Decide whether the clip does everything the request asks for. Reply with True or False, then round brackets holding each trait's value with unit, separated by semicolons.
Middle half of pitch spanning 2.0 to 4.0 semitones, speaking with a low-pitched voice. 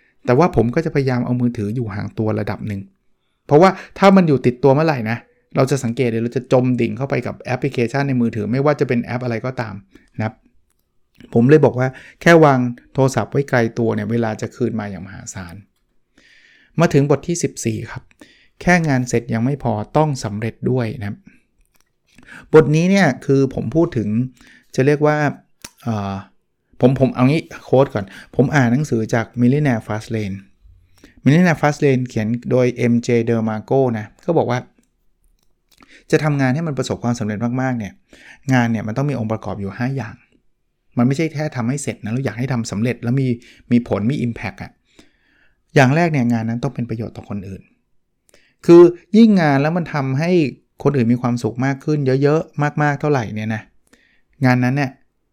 True (3.7 semitones; 125 Hz)